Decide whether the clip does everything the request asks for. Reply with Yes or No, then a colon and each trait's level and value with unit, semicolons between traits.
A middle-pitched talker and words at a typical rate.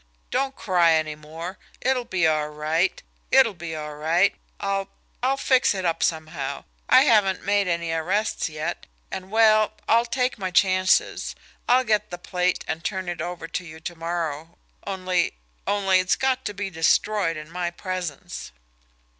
Yes: medium, 180 Hz; average, 165 wpm